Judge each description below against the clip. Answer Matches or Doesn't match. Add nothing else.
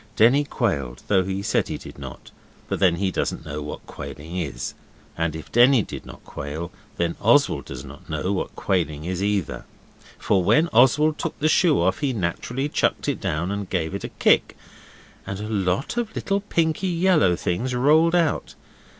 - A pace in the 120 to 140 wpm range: Doesn't match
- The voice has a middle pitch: Doesn't match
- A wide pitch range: Matches